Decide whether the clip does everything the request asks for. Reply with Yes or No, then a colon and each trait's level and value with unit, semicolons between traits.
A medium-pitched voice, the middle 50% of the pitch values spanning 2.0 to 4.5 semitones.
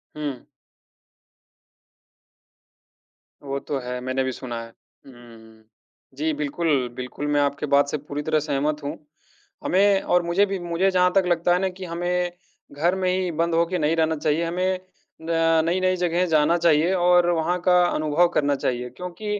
Yes: medium, 165 Hz; average, 3.8 semitones